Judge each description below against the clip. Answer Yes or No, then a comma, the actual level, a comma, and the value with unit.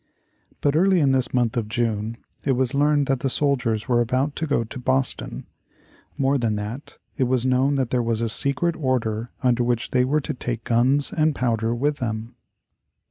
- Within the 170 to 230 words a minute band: Yes, average, 190 wpm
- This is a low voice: Yes, low, 125 Hz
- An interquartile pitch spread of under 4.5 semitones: Yes, average, 3.1 semitones